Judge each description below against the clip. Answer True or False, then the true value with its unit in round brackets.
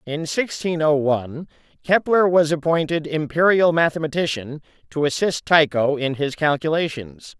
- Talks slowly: True (120 wpm)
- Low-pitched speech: False (155 Hz)